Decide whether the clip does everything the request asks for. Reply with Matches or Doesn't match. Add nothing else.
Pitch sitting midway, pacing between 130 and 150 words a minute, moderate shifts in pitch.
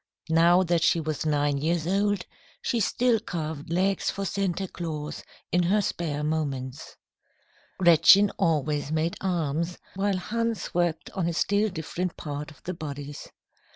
Matches